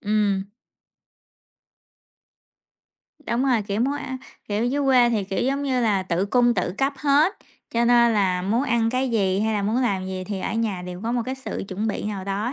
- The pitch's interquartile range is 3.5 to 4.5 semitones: Yes, average, 4.2 semitones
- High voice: Yes, high, 225 Hz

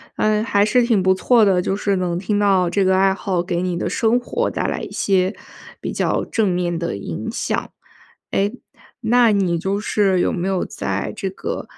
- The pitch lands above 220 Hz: No, high, 195 Hz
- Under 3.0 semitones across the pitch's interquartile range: Yes, narrow, 2.5 semitones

